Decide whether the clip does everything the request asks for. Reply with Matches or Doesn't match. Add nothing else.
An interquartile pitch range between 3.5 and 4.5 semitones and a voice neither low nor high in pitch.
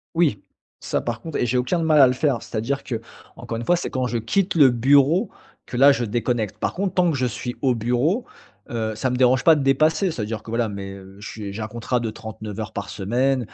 Doesn't match